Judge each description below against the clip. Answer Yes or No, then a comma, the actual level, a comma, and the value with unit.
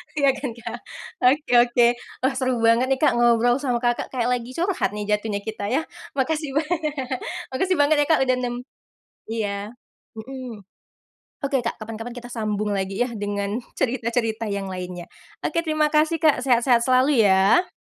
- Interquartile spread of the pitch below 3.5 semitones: No, average, 4.1 semitones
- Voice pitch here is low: No, high, 240 Hz